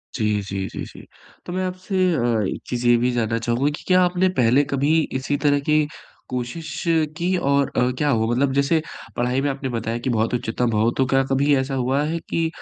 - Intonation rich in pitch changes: No, average, 3.6 semitones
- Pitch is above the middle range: No, low, 135 Hz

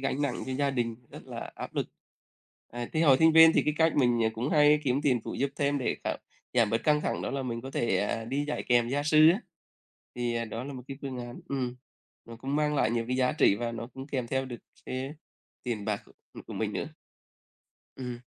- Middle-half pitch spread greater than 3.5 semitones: No, average, 3.2 semitones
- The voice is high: No, low, 130 Hz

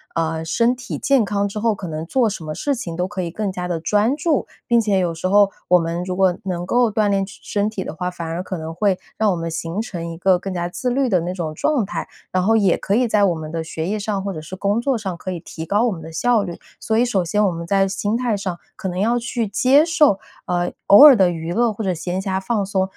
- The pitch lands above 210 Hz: No, high, 195 Hz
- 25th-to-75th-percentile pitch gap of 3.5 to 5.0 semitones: Yes, average, 4.0 semitones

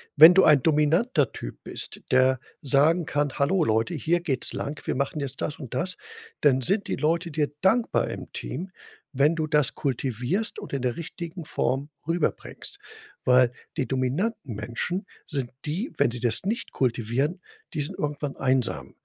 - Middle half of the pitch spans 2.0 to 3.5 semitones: No, average, 4.7 semitones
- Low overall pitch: No, medium, 145 Hz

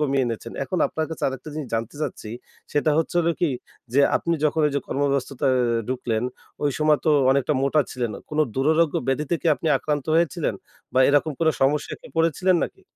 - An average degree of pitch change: Yes, average, 3.1 semitones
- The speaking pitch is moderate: Yes, medium, 145 Hz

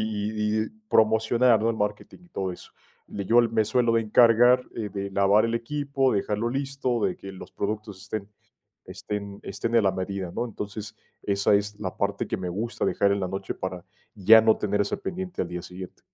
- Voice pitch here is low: Yes, low, 105 Hz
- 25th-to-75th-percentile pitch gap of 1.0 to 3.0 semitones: Yes, average, 2.7 semitones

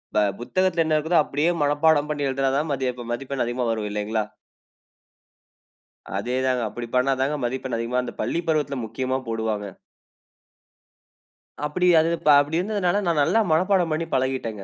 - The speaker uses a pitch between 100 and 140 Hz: Yes, low, 135 Hz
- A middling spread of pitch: Yes, average, 4.7 semitones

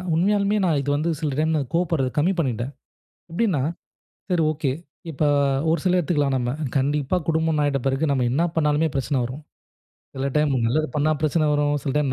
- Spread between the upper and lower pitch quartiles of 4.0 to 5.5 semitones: No, average, 2.9 semitones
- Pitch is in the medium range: Yes, medium, 150 Hz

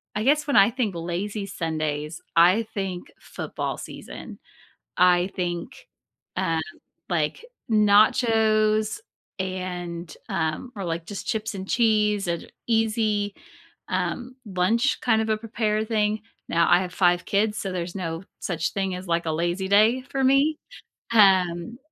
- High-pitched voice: Yes, high, 195 Hz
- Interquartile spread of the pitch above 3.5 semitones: Yes, average, 3.9 semitones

